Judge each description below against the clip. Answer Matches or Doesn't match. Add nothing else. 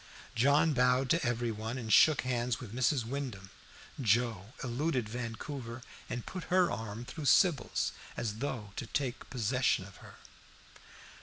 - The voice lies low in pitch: Matches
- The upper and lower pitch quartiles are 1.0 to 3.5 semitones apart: Matches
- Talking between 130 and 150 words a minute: Matches